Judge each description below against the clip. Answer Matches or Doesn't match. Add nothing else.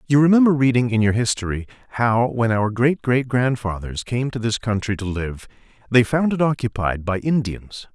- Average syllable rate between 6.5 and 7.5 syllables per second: Doesn't match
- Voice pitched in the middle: Doesn't match